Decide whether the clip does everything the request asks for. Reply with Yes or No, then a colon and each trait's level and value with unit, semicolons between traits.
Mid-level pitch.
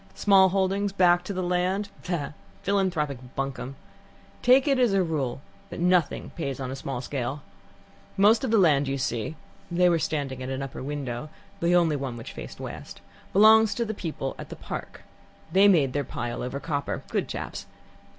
Yes: medium, 165 Hz